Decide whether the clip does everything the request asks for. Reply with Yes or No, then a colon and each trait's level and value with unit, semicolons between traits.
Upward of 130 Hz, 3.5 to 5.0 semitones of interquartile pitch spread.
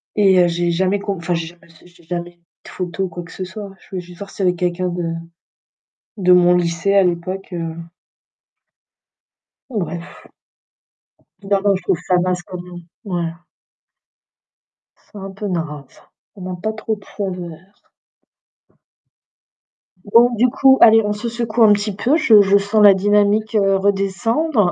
No: high, 190 Hz; average, 2.9 semitones